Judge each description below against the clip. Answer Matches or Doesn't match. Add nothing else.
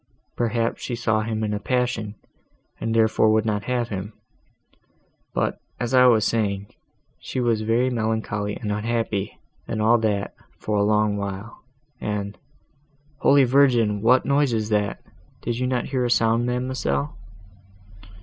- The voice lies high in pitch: Doesn't match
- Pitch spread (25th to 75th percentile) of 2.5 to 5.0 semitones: Matches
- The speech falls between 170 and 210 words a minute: Doesn't match